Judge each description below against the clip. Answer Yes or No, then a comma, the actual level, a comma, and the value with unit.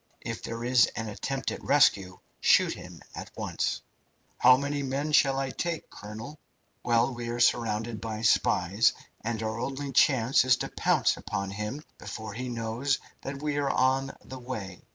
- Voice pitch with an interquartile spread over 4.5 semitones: No, average, 3.7 semitones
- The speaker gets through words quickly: No, average, 170 wpm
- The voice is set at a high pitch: No, low, 120 Hz